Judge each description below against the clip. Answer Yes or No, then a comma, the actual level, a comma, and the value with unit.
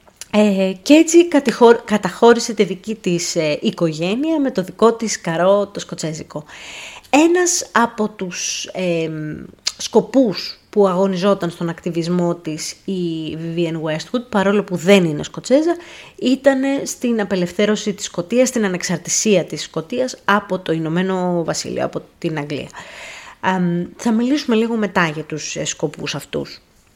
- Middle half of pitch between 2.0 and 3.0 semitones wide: No, average, 5.2 semitones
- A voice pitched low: No, high, 195 Hz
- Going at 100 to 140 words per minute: Yes, average, 135 wpm